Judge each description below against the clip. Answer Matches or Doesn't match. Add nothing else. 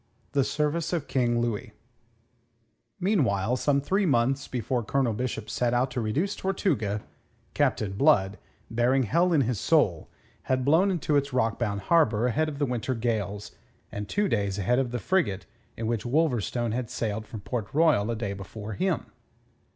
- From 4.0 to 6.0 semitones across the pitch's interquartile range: Matches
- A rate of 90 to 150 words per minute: Doesn't match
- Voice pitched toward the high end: Doesn't match